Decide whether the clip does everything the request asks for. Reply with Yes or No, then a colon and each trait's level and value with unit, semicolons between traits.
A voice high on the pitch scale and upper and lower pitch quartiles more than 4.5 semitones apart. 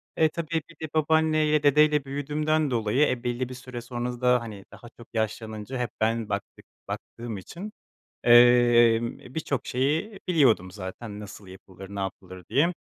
No: low, 125 Hz; average, 5.2 semitones